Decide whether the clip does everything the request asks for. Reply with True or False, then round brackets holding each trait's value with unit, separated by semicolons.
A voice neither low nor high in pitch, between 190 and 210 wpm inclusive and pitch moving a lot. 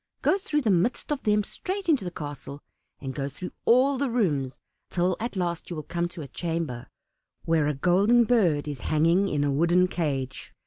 True (175 Hz; 195 wpm; 6.8 semitones)